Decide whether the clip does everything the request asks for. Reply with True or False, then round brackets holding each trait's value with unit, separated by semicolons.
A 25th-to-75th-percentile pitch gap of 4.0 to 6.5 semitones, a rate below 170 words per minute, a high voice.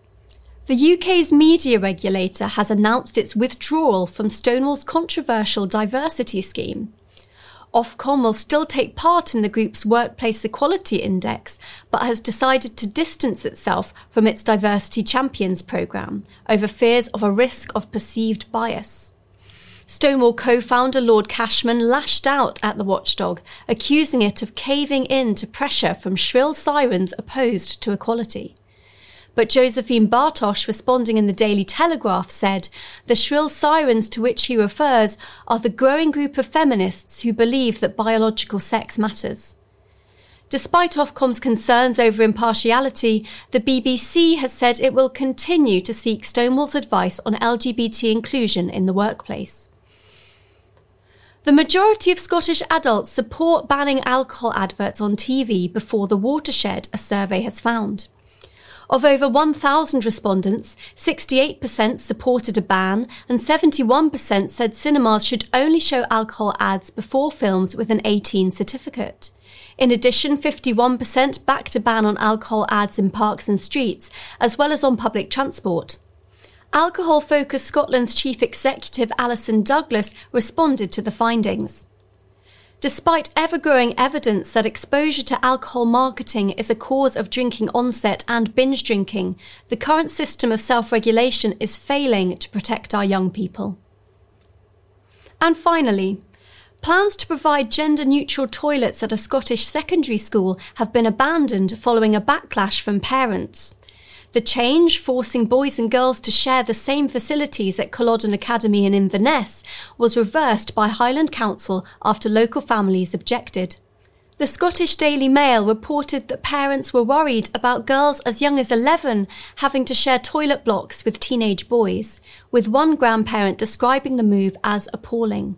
True (4.3 semitones; 140 wpm; 235 Hz)